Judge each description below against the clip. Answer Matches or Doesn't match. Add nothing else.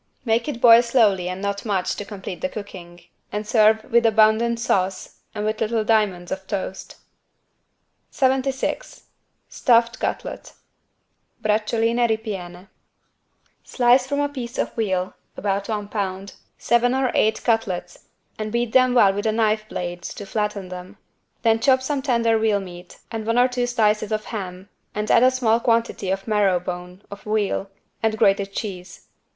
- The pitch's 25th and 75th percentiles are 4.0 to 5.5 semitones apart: Doesn't match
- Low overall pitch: Doesn't match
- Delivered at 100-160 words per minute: Matches